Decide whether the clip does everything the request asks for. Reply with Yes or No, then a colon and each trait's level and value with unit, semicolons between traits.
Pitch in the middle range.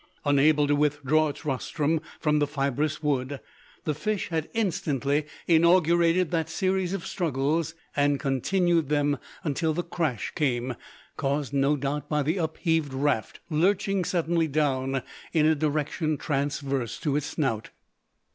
Yes: medium, 150 Hz